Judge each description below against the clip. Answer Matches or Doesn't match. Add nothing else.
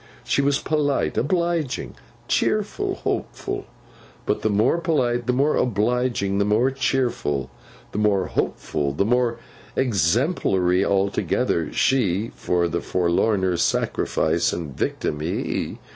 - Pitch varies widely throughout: Matches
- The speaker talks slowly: Matches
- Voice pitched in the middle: Doesn't match